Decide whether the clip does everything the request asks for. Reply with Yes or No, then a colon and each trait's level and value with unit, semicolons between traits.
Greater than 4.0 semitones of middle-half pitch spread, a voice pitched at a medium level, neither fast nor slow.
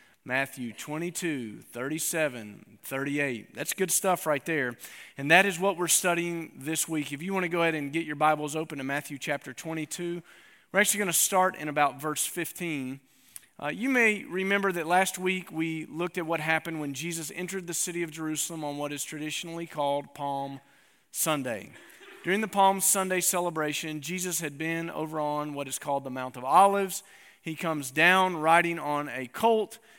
No: average, 3.6 semitones; medium, 160 Hz; average, 180 wpm